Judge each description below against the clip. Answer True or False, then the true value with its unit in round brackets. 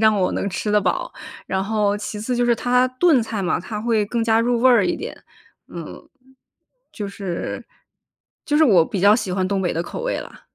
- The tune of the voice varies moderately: True (3.6 semitones)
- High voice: True (215 Hz)